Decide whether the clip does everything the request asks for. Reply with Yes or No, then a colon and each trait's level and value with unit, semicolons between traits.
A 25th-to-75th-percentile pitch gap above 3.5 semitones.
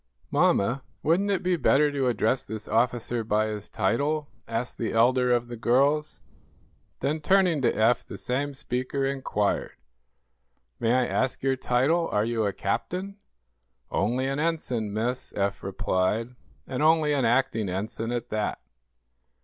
Yes: average, 4.2 semitones